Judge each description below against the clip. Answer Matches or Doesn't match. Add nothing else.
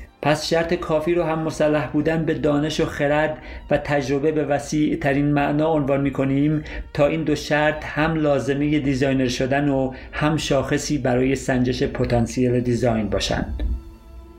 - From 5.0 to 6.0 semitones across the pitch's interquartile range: Doesn't match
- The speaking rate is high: Doesn't match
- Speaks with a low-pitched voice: Doesn't match